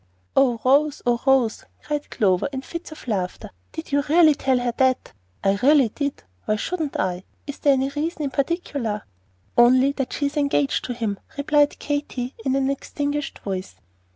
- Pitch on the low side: No, very high, 270 Hz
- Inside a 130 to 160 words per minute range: No, average, 175 wpm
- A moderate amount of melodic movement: Yes, average, 3.5 semitones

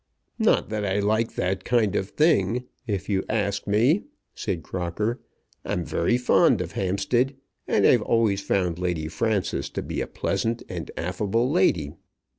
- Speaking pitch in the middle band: No, low, 100 Hz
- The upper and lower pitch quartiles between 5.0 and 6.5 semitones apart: No, average, 4.0 semitones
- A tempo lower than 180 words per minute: Yes, average, 155 wpm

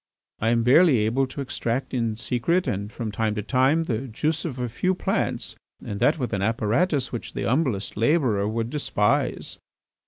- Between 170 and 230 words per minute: Yes, average, 180 wpm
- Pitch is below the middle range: Yes, low, 125 Hz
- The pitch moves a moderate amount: Yes, average, 4.5 semitones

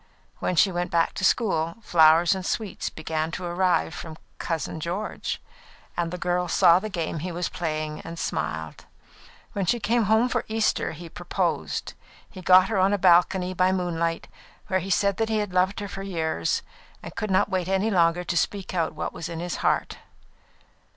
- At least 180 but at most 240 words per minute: Yes, average, 190 wpm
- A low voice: No, medium, 180 Hz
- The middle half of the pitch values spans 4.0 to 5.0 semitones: No, narrow, 2.6 semitones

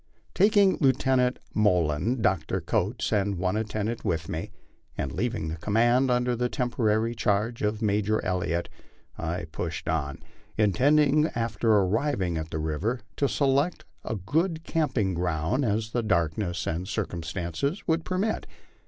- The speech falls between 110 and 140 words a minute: Yes, slow, 135 wpm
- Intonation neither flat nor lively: No, wide, 6.3 semitones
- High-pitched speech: No, low, 105 Hz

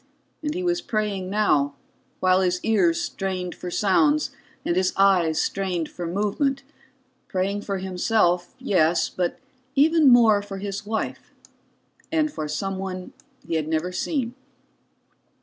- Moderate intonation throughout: Yes, average, 4.0 semitones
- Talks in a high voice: Yes, high, 195 Hz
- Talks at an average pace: No, slow, 130 wpm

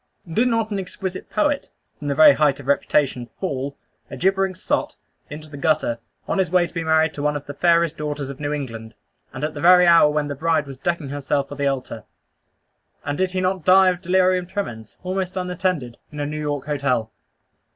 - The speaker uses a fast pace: Yes, fast, 210 wpm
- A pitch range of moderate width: Yes, average, 4.4 semitones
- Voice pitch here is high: No, medium, 150 Hz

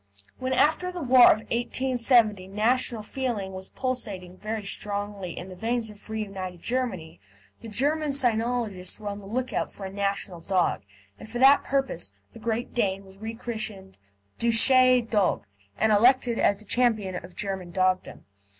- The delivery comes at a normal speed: Yes, average, 160 wpm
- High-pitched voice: Yes, high, 220 Hz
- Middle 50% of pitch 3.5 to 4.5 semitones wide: Yes, average, 4.1 semitones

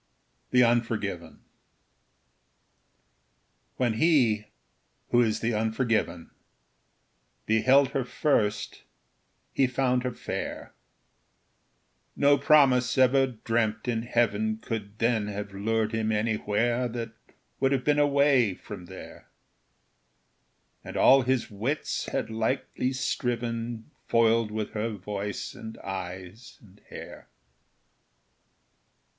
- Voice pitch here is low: Yes, low, 115 Hz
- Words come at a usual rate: No, slow, 100 wpm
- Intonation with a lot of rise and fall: No, average, 3.0 semitones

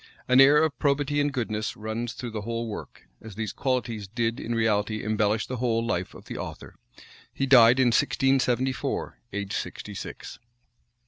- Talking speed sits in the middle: Yes, average, 170 wpm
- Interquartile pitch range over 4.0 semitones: No, average, 3.4 semitones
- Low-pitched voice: Yes, low, 115 Hz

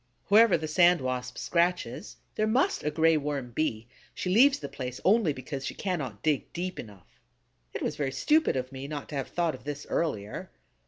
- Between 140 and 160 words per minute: No, average, 195 wpm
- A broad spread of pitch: Yes, wide, 5.8 semitones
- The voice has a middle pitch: Yes, medium, 150 Hz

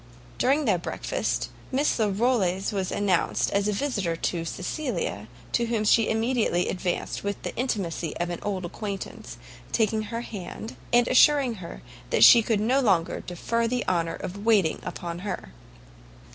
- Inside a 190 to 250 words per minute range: No, average, 150 wpm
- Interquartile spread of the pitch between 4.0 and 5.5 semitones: Yes, average, 4.7 semitones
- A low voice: No, high, 205 Hz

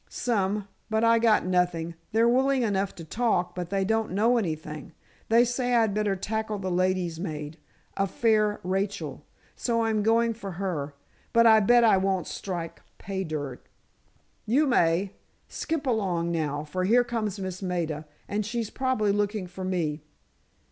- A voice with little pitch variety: No, average, 4.1 semitones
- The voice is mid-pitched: No, high, 200 Hz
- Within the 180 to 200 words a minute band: No, average, 160 wpm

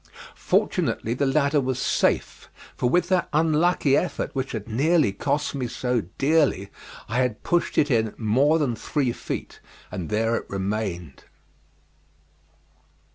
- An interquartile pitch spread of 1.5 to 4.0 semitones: No, average, 5.2 semitones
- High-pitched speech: No, low, 130 Hz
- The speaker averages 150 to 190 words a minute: No, slow, 135 wpm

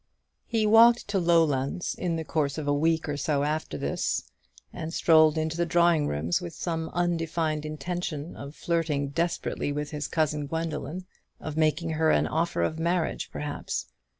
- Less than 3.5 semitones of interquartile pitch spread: Yes, narrow, 2.4 semitones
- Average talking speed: Yes, average, 165 wpm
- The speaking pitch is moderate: Yes, medium, 160 Hz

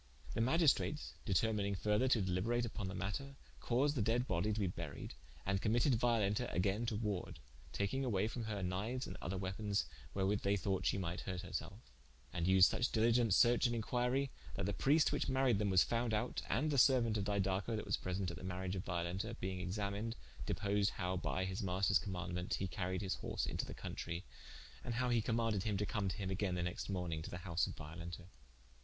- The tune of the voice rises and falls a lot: No, average, 3.9 semitones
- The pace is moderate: No, fast, 210 wpm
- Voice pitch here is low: Yes, low, 100 Hz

